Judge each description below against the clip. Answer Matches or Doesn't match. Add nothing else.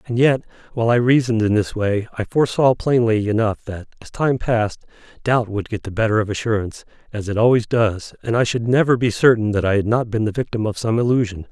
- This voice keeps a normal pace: Doesn't match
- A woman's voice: Doesn't match